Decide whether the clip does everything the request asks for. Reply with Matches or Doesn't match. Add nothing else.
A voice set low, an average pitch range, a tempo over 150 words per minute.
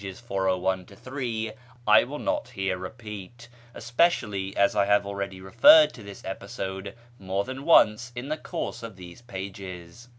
Doesn't match